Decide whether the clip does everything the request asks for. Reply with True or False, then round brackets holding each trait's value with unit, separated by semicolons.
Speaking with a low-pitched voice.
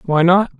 False (175 Hz)